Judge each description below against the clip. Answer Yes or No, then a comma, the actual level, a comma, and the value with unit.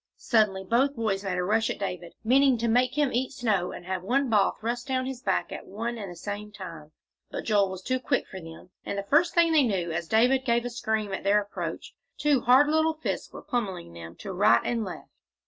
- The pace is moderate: No, fast, 235 wpm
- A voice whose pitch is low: No, high, 220 Hz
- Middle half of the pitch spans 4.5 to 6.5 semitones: Yes, average, 5.0 semitones